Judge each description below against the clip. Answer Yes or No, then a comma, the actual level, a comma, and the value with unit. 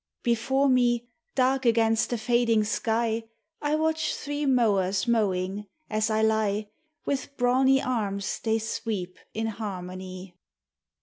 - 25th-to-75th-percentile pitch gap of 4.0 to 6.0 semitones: No, average, 3.4 semitones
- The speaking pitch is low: No, high, 225 Hz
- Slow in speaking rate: Yes, slow, 120 wpm